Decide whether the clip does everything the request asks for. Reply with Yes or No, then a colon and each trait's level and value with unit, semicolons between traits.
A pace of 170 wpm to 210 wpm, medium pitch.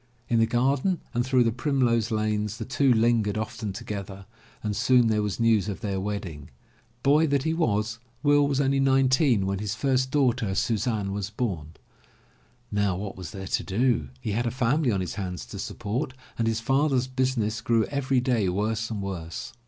No: average, 190 wpm; low, 115 Hz